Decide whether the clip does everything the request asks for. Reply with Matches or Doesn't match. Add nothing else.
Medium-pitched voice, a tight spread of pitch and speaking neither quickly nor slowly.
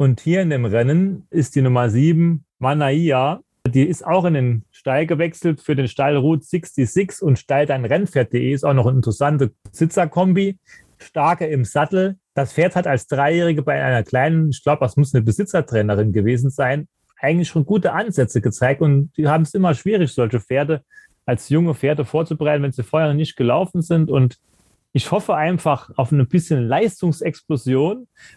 Doesn't match